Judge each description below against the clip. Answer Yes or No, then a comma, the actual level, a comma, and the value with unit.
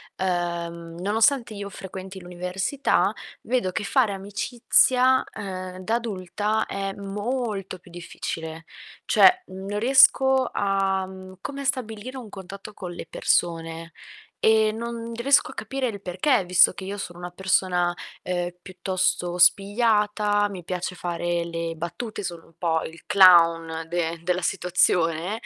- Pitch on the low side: No, high, 190 Hz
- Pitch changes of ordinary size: Yes, average, 3.5 semitones